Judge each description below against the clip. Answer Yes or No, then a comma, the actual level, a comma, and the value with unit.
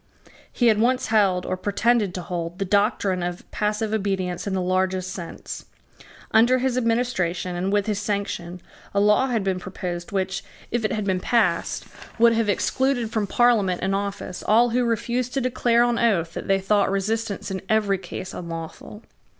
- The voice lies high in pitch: Yes, high, 200 Hz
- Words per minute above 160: Yes, average, 175 wpm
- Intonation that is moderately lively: Yes, average, 3.7 semitones